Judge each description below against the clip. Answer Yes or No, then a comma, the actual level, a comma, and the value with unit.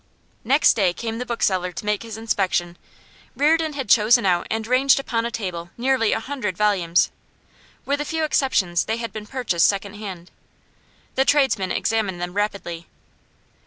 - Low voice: No, high, 215 Hz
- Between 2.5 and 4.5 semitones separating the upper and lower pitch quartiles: No, wide, 5.4 semitones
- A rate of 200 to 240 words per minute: No, average, 160 wpm